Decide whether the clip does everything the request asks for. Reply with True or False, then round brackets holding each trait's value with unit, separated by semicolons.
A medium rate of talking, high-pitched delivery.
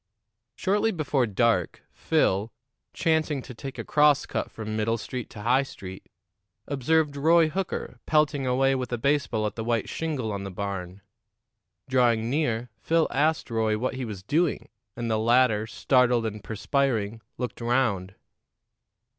False (150 wpm; 125 Hz)